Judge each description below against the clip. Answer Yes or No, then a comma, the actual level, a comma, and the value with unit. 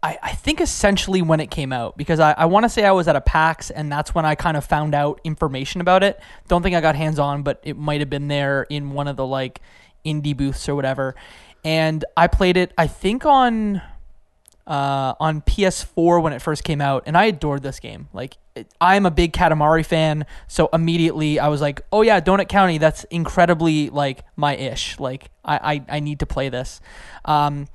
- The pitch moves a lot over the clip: No, average, 3.2 semitones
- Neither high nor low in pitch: Yes, medium, 155 Hz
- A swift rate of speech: Yes, fast, 215 wpm